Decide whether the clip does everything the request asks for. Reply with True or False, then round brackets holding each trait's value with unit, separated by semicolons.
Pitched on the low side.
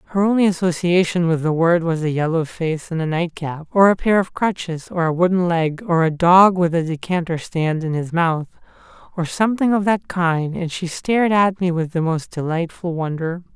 False (170 Hz)